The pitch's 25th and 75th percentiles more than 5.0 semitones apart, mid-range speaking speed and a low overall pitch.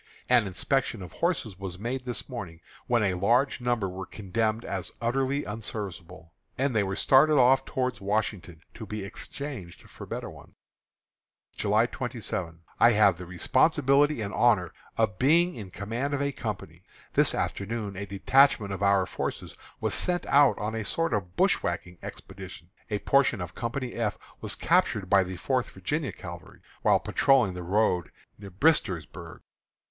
Yes: wide, 5.4 semitones; average, 160 wpm; low, 105 Hz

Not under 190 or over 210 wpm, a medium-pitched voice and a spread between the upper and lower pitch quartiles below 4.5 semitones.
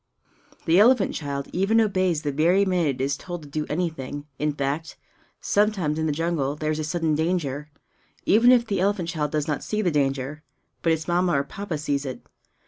Yes: average, 200 wpm; medium, 160 Hz; average, 4.0 semitones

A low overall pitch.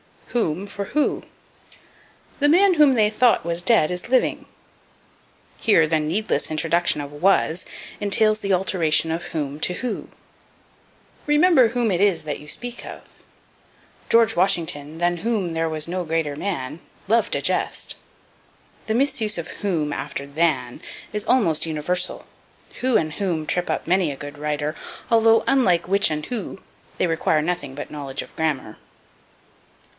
No: medium, 175 Hz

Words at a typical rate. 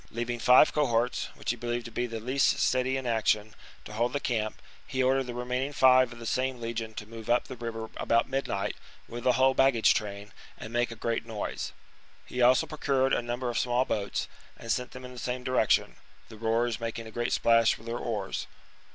No: fast, 220 wpm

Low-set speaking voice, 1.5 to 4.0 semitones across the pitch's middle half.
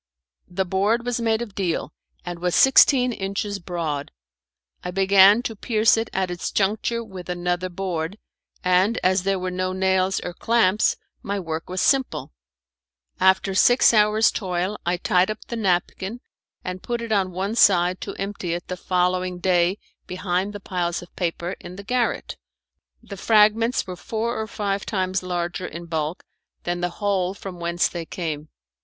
No: high, 190 Hz; average, 2.9 semitones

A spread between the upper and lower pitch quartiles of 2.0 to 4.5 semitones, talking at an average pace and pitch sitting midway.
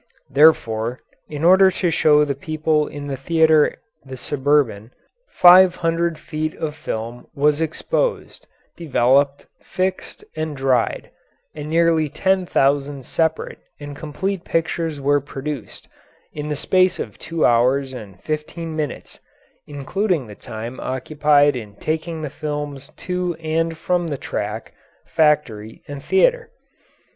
No: average, 3.3 semitones; slow, 130 wpm; medium, 150 Hz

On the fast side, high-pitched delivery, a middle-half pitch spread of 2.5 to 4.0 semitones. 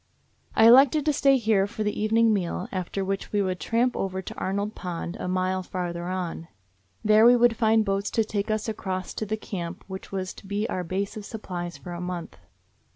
Yes: fast, 210 wpm; high, 200 Hz; average, 3.0 semitones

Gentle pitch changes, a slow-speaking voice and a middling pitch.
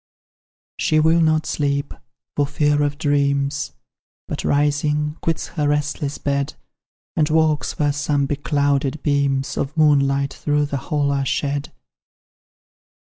Yes: narrow, 1.2 semitones; slow, 125 wpm; medium, 145 Hz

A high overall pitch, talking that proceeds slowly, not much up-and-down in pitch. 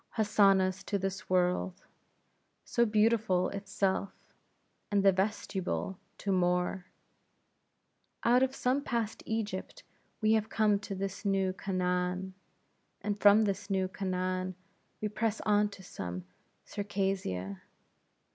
Yes: high, 195 Hz; slow, 115 wpm; narrow, 2.2 semitones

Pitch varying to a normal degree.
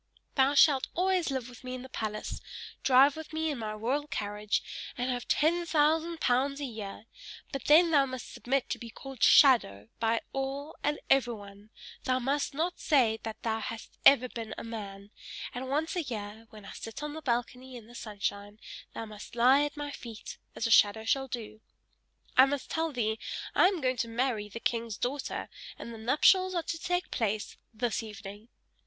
Yes: average, 4.5 semitones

